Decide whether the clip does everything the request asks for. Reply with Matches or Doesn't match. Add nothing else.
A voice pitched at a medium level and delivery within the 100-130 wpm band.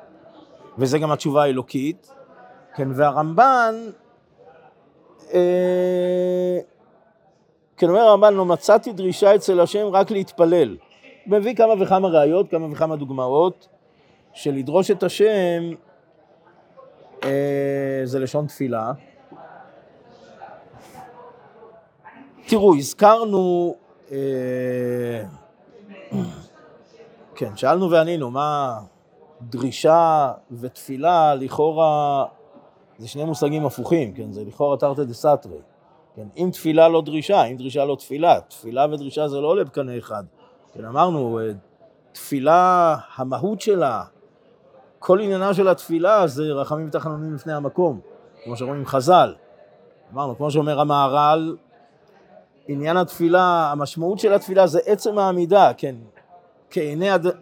Matches